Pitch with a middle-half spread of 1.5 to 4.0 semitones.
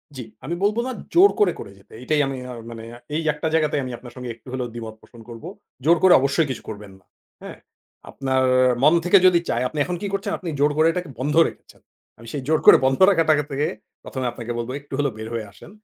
No: wide, 5.4 semitones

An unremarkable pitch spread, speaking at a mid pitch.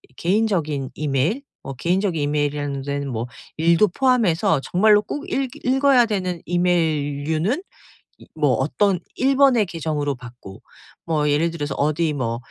No: wide, 6.1 semitones; medium, 160 Hz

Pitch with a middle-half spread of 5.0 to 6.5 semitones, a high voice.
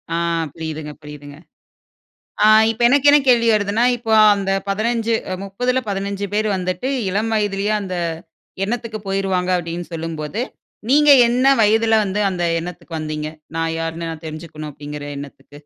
Yes: average, 5.3 semitones; high, 195 Hz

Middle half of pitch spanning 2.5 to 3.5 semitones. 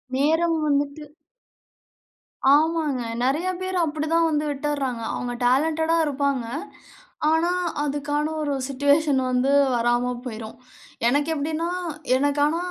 Yes: average, 2.9 semitones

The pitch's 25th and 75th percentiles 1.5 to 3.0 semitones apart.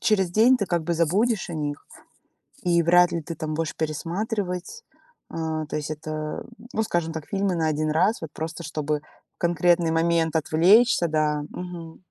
Yes: narrow, 2.6 semitones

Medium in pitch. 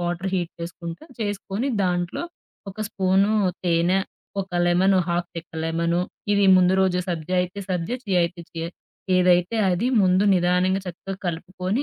Yes: medium, 180 Hz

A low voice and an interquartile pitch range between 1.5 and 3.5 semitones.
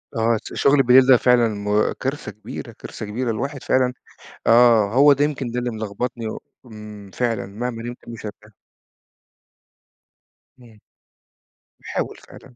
Yes: low, 120 Hz; average, 2.7 semitones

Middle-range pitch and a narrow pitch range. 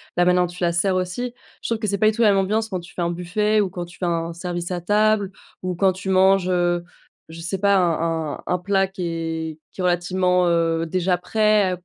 Yes: medium, 180 Hz; narrow, 2.2 semitones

